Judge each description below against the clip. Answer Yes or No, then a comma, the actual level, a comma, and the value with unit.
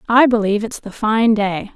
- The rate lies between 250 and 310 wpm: No, fast, 205 wpm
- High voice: Yes, high, 220 Hz